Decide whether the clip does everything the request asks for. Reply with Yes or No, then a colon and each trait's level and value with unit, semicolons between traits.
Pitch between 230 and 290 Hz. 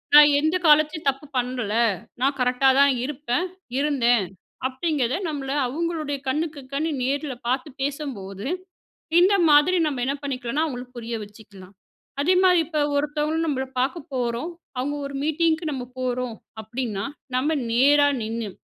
Yes: very high, 275 Hz